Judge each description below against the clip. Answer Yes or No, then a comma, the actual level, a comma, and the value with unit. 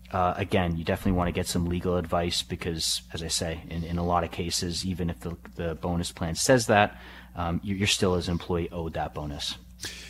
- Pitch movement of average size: No, narrow, 1.4 semitones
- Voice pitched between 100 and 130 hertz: No, very low, 85 Hz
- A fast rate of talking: Yes, fast, 220 wpm